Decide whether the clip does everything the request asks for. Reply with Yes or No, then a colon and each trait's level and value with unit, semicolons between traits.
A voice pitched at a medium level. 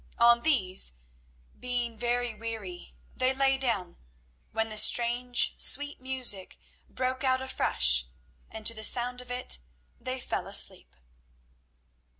No: high, 240 Hz